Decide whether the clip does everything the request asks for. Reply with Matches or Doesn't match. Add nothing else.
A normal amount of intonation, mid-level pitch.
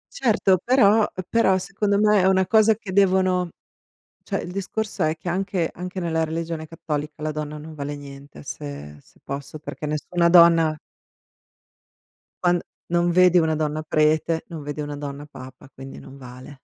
Matches